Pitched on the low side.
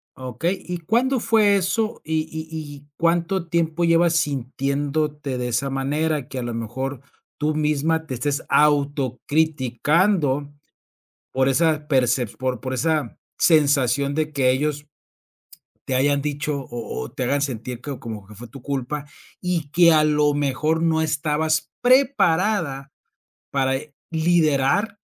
No: medium, 150 Hz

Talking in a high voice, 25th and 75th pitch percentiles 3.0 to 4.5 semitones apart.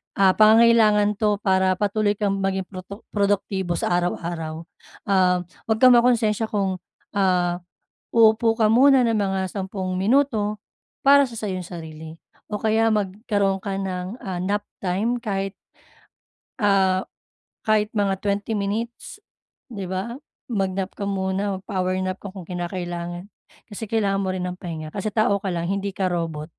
No: high, 195 Hz; narrow, 2.5 semitones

